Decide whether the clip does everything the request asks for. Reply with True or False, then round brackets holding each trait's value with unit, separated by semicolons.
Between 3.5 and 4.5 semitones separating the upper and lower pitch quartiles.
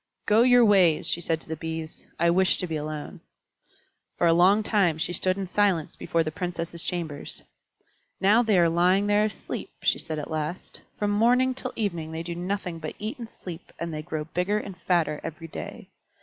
True (4.0 semitones)